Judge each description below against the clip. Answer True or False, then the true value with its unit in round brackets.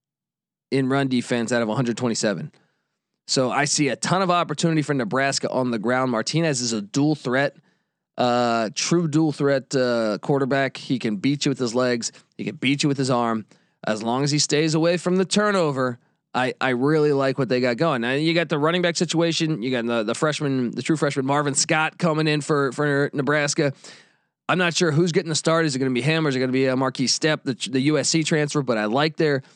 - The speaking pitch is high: False (140 Hz)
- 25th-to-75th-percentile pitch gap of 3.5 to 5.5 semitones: True (3.8 semitones)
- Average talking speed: False (225 wpm)